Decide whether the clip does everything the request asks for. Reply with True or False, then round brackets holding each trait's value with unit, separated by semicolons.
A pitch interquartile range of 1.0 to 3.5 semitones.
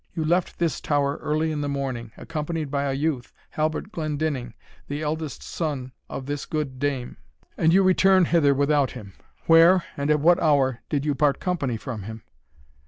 True (2.8 semitones)